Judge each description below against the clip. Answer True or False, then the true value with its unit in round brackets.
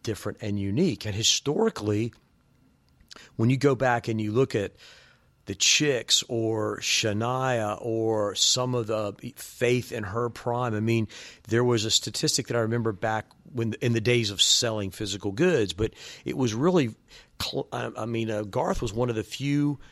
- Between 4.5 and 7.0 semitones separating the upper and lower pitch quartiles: False (2.5 semitones)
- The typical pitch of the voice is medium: False (115 Hz)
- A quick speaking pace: False (165 wpm)